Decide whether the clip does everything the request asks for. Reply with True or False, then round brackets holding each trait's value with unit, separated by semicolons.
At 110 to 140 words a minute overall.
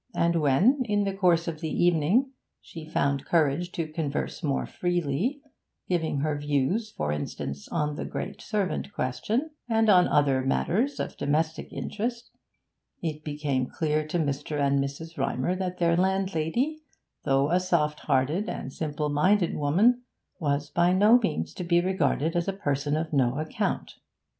False (155 wpm)